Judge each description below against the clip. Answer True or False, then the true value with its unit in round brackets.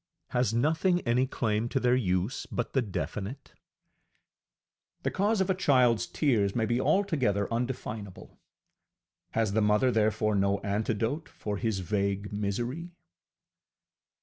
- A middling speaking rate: False (125 wpm)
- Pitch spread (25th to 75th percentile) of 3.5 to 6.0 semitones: True (4.2 semitones)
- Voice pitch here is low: True (115 Hz)